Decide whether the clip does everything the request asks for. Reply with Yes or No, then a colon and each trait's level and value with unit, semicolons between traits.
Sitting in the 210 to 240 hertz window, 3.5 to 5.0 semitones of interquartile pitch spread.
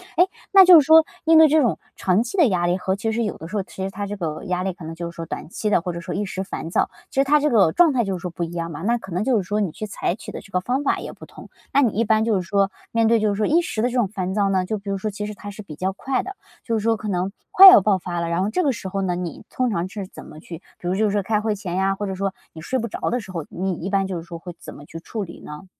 No: high, 195 Hz; average, 3.8 semitones